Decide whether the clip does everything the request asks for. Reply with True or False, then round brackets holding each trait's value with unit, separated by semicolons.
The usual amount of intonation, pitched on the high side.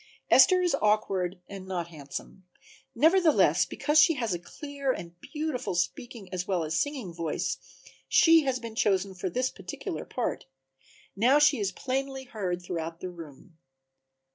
False (7.7 semitones; 210 Hz)